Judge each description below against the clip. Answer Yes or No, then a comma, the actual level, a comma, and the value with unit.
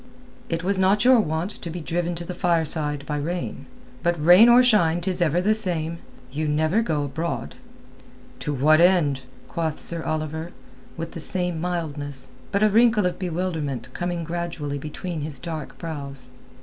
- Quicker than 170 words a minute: No, average, 165 wpm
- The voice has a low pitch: No, medium, 165 Hz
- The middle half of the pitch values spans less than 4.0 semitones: Yes, average, 2.9 semitones